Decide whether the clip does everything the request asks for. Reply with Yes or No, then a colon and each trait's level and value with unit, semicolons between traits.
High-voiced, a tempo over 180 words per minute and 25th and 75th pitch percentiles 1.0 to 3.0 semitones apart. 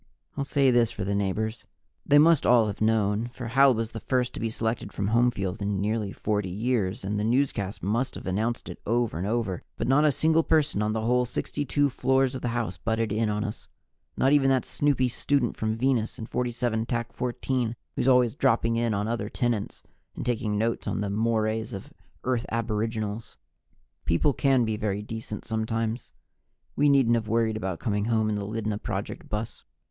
No: low, 115 Hz; average, 195 wpm; average, 2.7 semitones